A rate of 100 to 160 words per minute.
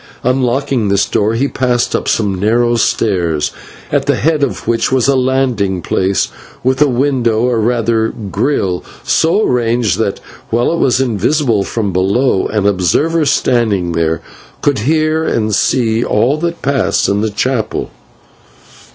Yes: average, 150 wpm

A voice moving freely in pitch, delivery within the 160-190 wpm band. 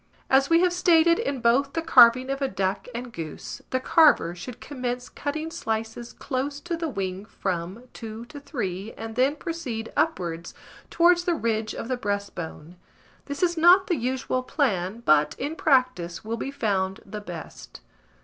Yes: wide, 6.4 semitones; average, 170 wpm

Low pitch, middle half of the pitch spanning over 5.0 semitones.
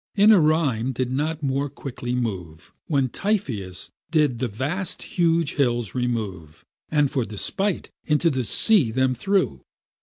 Yes: low, 130 Hz; wide, 5.6 semitones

